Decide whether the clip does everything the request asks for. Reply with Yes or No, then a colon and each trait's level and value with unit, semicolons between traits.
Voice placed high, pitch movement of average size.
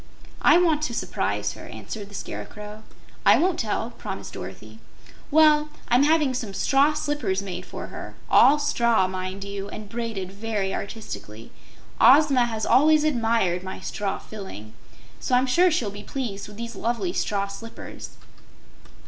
No: high, 220 Hz; wide, 5.8 semitones